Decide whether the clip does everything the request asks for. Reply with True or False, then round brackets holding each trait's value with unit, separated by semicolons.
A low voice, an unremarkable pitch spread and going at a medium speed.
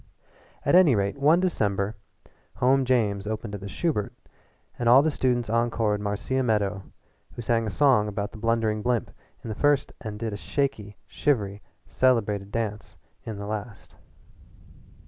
True (110 Hz; 3.6 semitones; 160 wpm)